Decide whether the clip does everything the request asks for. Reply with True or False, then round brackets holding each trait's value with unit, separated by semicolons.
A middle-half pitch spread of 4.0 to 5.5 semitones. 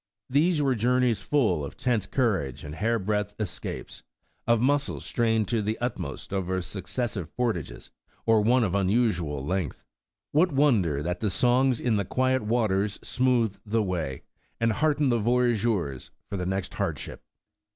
True (4.8 semitones)